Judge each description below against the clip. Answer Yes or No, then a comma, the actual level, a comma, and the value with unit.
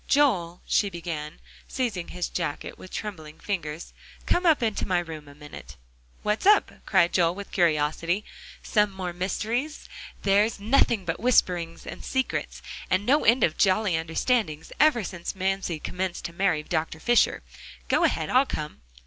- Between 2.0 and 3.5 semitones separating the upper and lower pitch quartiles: No, average, 4.6 semitones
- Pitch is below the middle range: No, medium, 185 Hz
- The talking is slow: No, average, 155 wpm